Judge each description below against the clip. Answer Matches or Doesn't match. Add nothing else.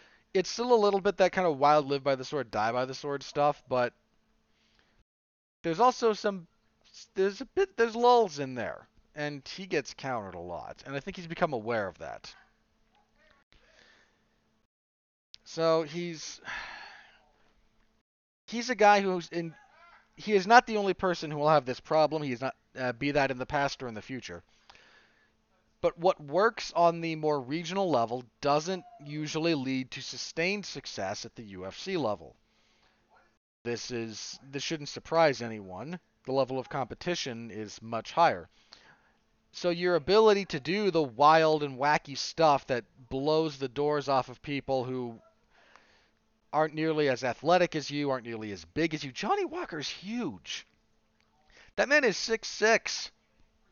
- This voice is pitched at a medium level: Matches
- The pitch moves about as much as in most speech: Doesn't match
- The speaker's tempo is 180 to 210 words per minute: Doesn't match